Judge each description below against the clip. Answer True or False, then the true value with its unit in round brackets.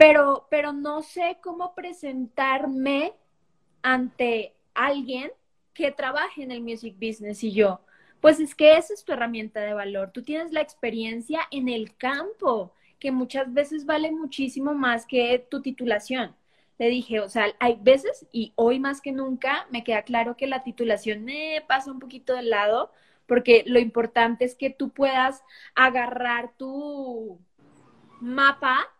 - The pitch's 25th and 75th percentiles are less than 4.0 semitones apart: True (3.6 semitones)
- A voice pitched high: True (260 Hz)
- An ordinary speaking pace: True (155 wpm)